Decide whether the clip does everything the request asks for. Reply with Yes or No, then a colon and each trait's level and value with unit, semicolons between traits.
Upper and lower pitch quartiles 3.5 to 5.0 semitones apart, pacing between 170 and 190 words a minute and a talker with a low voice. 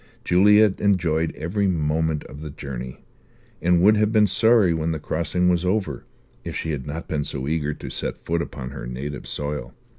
Yes: average, 4.0 semitones; average, 185 wpm; very low, 80 Hz